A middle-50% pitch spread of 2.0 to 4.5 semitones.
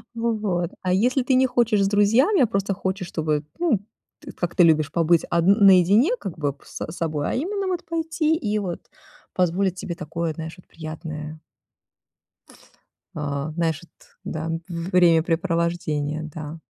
No: average, 5.0 semitones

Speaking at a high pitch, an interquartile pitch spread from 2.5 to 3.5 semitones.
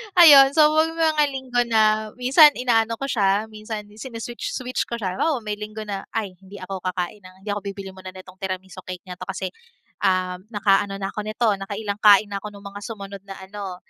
Yes: high, 205 Hz; average, 3.2 semitones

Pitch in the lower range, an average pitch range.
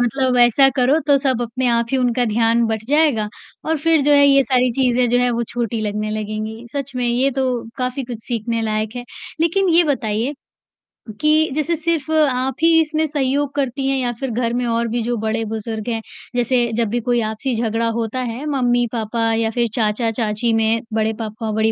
No: high, 240 Hz; average, 3.1 semitones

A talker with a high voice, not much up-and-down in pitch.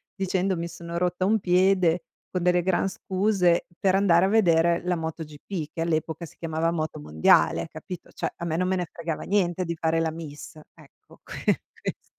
No: medium, 170 Hz; narrow, 2.2 semitones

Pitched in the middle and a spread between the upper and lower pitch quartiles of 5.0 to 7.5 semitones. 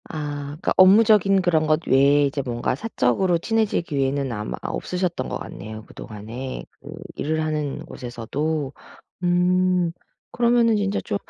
Yes: medium, 155 Hz; average, 5.3 semitones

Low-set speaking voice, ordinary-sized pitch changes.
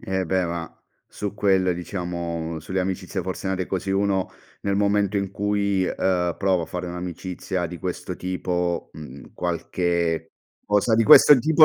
No: very low, 95 Hz; narrow, 2.2 semitones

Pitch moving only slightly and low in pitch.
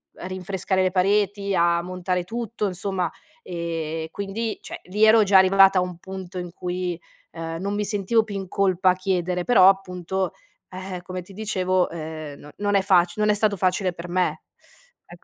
No: narrow, 2.0 semitones; medium, 185 Hz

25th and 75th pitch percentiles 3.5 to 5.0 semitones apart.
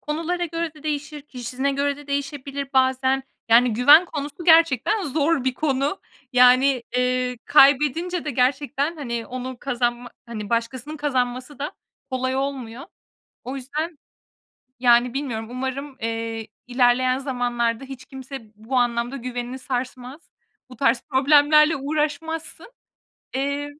No: average, 2.9 semitones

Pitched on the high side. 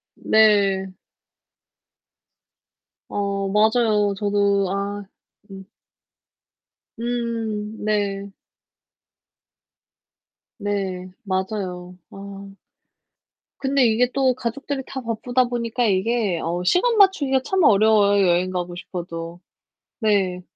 Yes: high, 205 Hz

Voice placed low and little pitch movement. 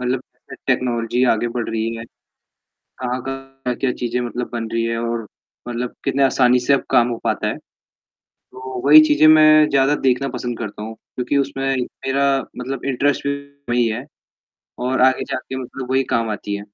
Yes: low, 125 Hz; narrow, 2.2 semitones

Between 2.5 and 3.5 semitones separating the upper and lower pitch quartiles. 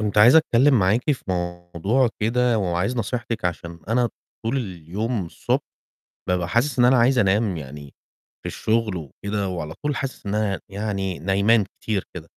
No: average, 4.8 semitones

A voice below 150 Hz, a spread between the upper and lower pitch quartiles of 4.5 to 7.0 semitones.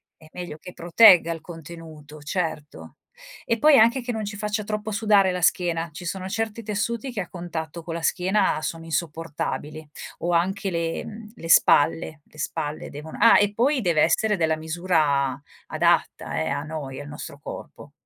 No: medium, 170 Hz; average, 4.8 semitones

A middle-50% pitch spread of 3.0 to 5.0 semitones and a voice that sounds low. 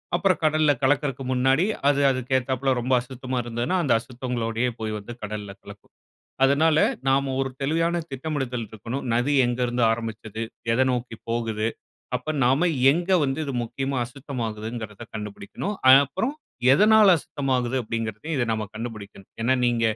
Yes: average, 3.4 semitones; low, 125 Hz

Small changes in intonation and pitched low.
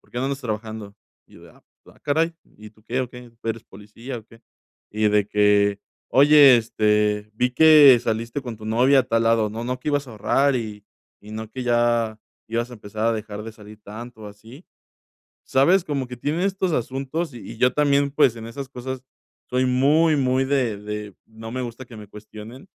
No: average, 3.8 semitones; low, 120 Hz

